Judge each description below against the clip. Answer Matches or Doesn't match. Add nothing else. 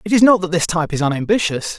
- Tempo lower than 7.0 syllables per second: Doesn't match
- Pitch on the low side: Doesn't match